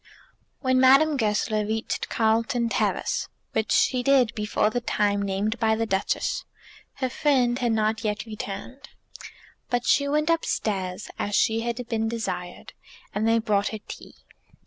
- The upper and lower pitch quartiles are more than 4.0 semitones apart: No, average, 2.8 semitones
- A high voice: Yes, high, 225 Hz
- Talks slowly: No, average, 145 wpm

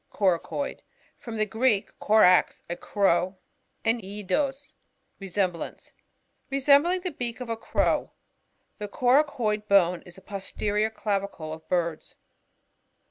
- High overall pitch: Yes, high, 210 Hz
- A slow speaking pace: Yes, slow, 115 wpm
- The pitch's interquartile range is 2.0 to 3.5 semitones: No, average, 4.6 semitones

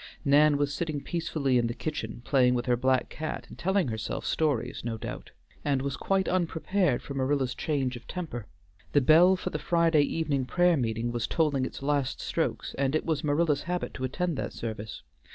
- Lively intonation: No, average, 4.4 semitones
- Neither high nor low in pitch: Yes, medium, 145 Hz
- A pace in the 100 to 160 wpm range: No, average, 190 wpm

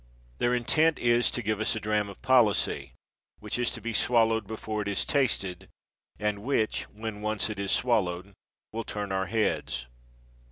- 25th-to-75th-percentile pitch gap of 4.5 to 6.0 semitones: No, narrow, 2.6 semitones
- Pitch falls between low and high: No, low, 110 Hz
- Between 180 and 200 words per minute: No, average, 170 wpm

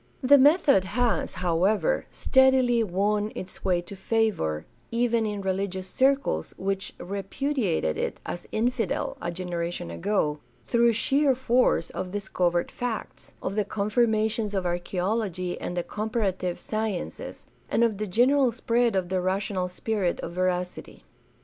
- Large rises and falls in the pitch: No, average, 4.3 semitones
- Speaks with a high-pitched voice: Yes, high, 200 Hz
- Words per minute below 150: Yes, average, 140 wpm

